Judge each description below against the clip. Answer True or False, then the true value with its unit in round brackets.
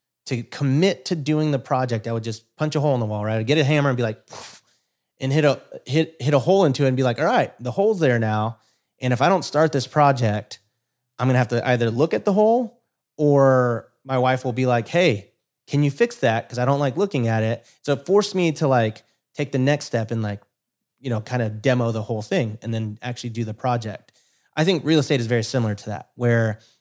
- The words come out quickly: True (250 wpm)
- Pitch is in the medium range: False (125 Hz)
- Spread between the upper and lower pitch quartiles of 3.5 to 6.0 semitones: True (4.2 semitones)